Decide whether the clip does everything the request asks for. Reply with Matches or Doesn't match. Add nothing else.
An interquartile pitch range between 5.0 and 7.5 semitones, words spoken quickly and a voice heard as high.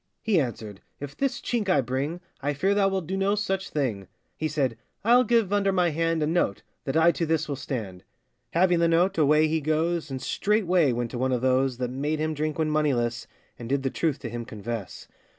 Doesn't match